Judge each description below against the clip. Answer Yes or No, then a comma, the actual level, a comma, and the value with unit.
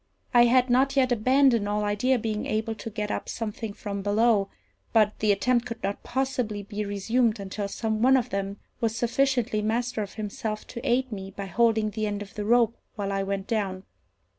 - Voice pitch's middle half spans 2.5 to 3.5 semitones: Yes, average, 2.8 semitones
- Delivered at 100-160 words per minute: No, average, 200 wpm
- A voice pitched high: Yes, high, 220 Hz